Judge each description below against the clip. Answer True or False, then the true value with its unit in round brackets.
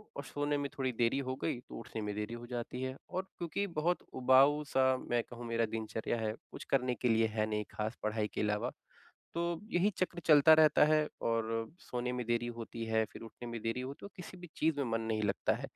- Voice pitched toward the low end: True (120 Hz)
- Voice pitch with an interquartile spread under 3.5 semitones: False (4.3 semitones)